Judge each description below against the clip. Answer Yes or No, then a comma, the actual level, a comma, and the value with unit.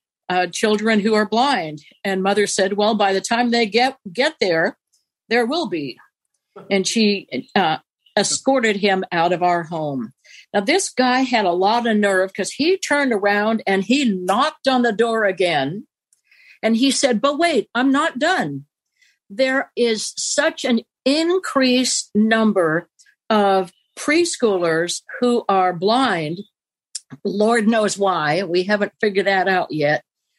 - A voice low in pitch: No, high, 220 Hz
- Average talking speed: Yes, average, 150 wpm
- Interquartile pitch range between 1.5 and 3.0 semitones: No, average, 5.1 semitones